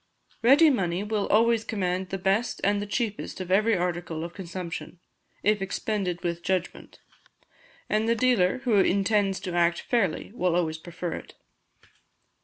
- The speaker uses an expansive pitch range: No, average, 3.4 semitones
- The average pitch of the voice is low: No, high, 195 Hz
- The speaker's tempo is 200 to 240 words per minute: No, average, 145 wpm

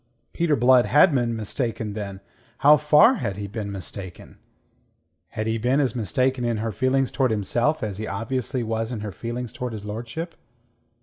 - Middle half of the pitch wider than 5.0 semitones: No, average, 3.6 semitones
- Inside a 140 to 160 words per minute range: No, average, 175 wpm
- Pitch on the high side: No, low, 115 Hz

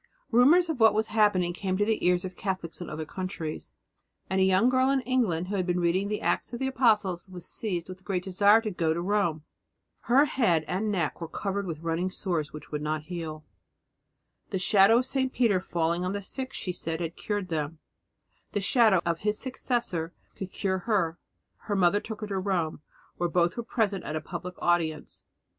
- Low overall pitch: No, medium, 185 Hz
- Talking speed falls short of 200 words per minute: No, fast, 205 wpm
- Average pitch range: Yes, average, 3.8 semitones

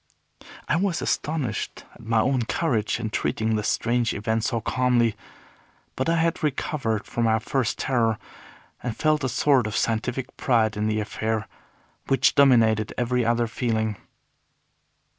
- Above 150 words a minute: No, average, 145 wpm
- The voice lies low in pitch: Yes, low, 115 Hz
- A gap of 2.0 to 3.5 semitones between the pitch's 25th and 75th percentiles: Yes, average, 3.1 semitones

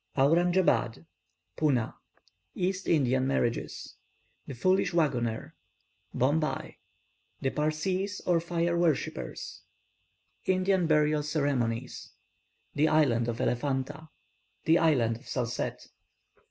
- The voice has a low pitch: No, medium, 150 Hz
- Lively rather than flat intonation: No, average, 5.0 semitones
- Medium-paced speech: No, slow, 90 wpm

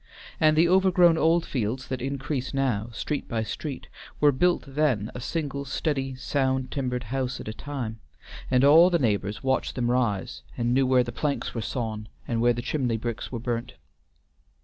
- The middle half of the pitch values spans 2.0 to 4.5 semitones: Yes, average, 3.4 semitones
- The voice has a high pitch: No, low, 130 Hz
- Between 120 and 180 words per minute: Yes, average, 175 wpm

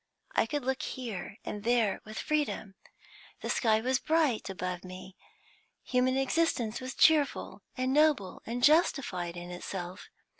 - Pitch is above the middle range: Yes, high, 240 Hz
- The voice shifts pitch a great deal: Yes, wide, 5.9 semitones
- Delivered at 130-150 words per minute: Yes, average, 140 wpm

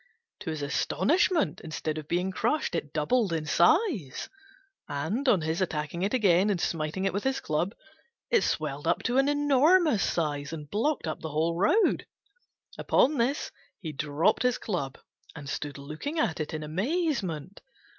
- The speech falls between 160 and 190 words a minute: Yes, average, 165 wpm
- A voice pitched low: No, medium, 175 Hz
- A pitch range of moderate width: No, wide, 8.6 semitones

